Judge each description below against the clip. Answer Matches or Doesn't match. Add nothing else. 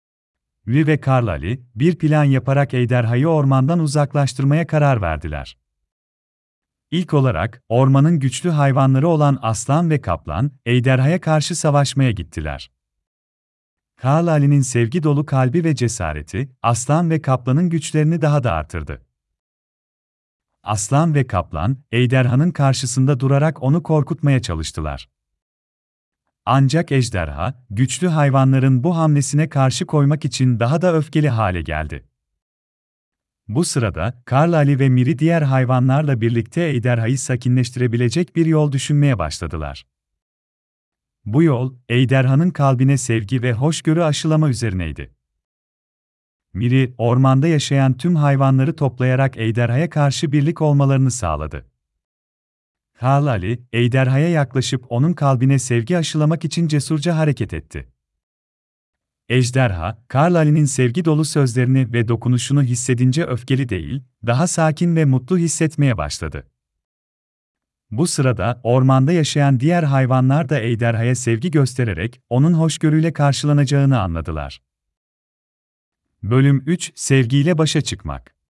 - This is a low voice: Matches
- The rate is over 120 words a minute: Doesn't match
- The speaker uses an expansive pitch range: Matches